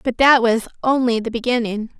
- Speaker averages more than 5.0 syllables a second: Yes, 5.5 syllables/s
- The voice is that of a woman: Yes, female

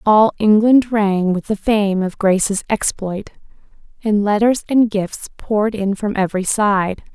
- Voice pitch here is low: No, high, 205 Hz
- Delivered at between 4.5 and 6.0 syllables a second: No, 4.2 syllables/s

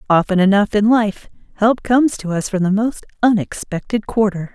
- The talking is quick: No, average, 170 wpm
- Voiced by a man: No, female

